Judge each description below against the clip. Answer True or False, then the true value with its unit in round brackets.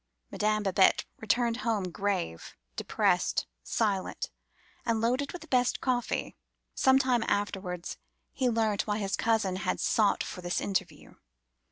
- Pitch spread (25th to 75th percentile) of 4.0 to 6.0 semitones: False (3.6 semitones)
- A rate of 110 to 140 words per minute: True (135 wpm)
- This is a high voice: True (215 Hz)